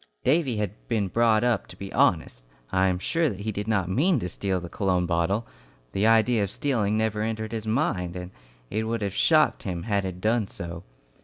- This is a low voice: Yes, low, 105 Hz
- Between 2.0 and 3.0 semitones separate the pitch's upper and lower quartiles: No, average, 3.5 semitones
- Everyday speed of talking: No, fast, 210 wpm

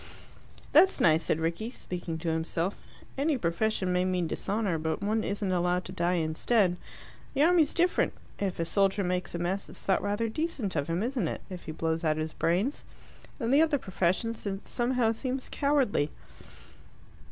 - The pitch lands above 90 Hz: Yes, high, 190 Hz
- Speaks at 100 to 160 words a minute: No, average, 175 wpm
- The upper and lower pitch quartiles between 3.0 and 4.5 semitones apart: No, wide, 5.6 semitones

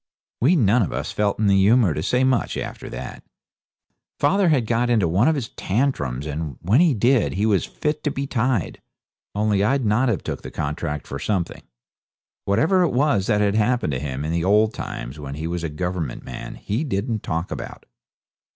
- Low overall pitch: Yes, low, 105 Hz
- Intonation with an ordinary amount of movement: No, wide, 6.9 semitones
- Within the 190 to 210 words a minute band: Yes, average, 200 wpm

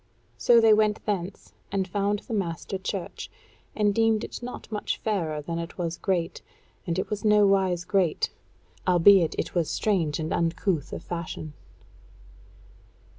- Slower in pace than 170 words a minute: Yes, average, 145 wpm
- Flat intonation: No, average, 3.7 semitones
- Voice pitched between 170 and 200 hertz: Yes, high, 190 Hz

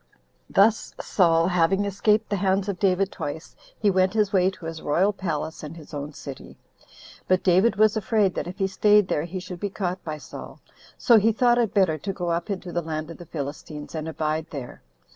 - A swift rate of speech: Yes, fast, 215 wpm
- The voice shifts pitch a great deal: No, average, 3.8 semitones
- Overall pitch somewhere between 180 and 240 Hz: Yes, medium, 185 Hz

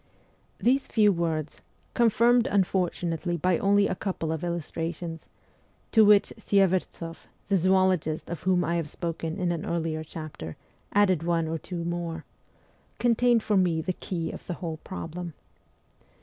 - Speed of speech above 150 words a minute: No, average, 145 wpm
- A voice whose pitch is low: No, medium, 175 Hz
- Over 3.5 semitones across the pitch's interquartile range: No, average, 2.9 semitones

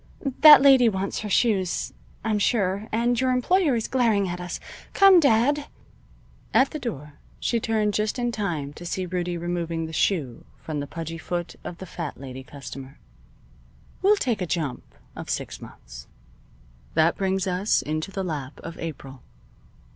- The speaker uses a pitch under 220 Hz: Yes, medium, 185 Hz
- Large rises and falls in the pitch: Yes, wide, 6.3 semitones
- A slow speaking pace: No, average, 160 wpm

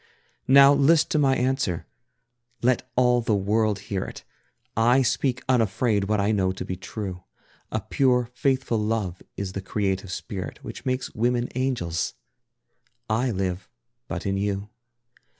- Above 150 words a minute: No, average, 145 wpm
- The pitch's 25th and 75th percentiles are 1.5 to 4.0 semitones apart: No, average, 4.5 semitones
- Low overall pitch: Yes, low, 110 Hz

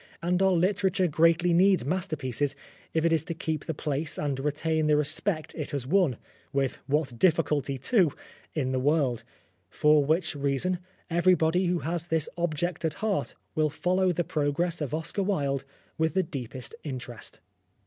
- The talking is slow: No, average, 165 wpm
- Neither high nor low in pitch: Yes, medium, 160 Hz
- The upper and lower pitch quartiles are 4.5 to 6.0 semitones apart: No, average, 3.6 semitones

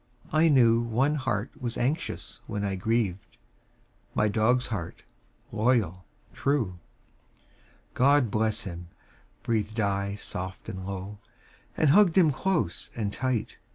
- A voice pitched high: No, low, 110 Hz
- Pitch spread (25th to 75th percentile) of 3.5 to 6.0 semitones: Yes, average, 4.7 semitones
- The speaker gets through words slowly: Yes, slow, 120 wpm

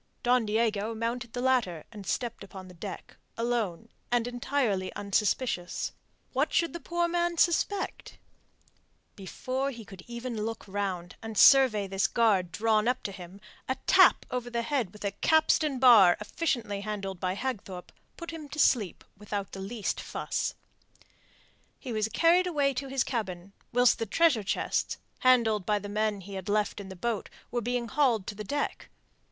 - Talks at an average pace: Yes, average, 170 wpm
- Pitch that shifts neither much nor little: Yes, average, 4.3 semitones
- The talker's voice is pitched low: No, high, 225 Hz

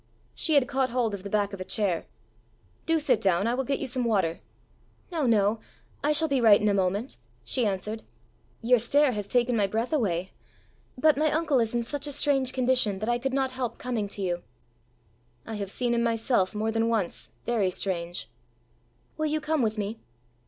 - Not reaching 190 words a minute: No, average, 200 wpm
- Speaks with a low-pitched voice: No, high, 230 Hz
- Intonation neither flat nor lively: Yes, average, 4.6 semitones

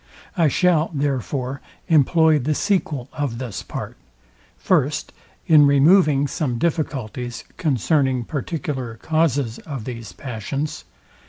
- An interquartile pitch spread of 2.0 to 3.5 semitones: No, average, 3.9 semitones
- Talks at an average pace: No, slow, 105 wpm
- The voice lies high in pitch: No, medium, 140 Hz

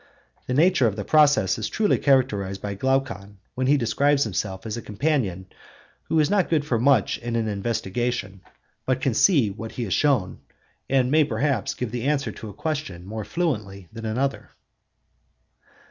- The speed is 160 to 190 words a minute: Yes, average, 175 wpm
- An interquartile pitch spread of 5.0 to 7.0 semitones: Yes, wide, 5.4 semitones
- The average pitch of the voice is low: Yes, low, 120 Hz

